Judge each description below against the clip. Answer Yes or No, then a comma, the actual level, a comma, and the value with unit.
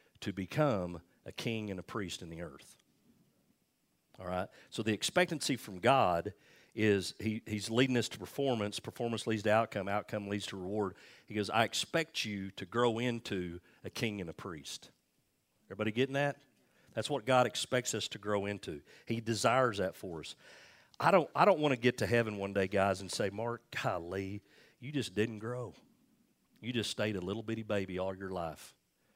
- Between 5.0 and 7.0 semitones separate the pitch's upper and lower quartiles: No, average, 3.5 semitones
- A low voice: Yes, low, 110 Hz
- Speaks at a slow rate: No, average, 185 wpm